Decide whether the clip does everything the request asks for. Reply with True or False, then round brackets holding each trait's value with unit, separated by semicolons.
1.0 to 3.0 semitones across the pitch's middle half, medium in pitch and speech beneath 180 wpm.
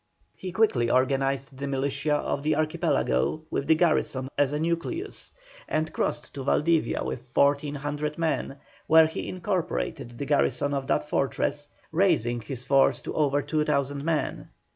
True (2.5 semitones; 145 Hz; 145 wpm)